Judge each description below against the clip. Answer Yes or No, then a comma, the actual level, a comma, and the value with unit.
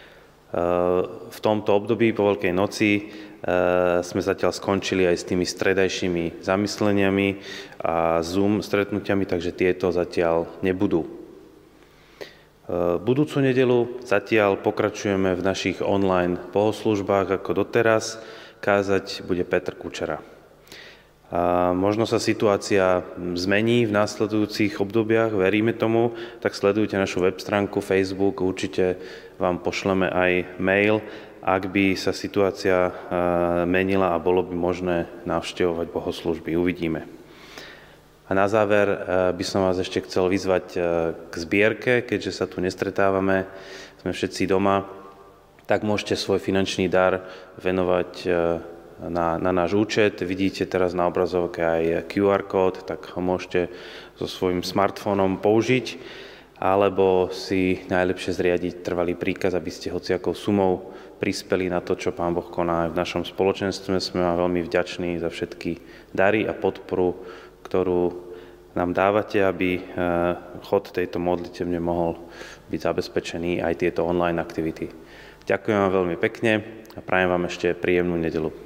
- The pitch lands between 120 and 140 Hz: No, very low, 95 Hz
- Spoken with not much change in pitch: Yes, narrow, 2.0 semitones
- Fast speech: No, average, 125 wpm